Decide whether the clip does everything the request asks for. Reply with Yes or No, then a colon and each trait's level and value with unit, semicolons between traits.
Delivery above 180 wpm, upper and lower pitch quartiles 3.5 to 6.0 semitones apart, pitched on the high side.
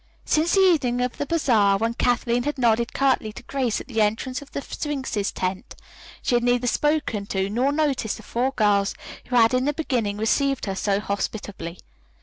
Yes: average, 190 wpm; average, 4.7 semitones; high, 240 Hz